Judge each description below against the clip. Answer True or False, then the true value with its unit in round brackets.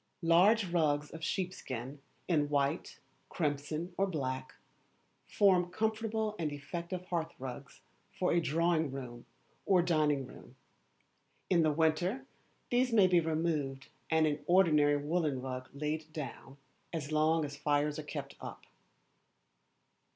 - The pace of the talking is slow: True (130 wpm)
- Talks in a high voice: False (155 Hz)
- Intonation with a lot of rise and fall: False (3.5 semitones)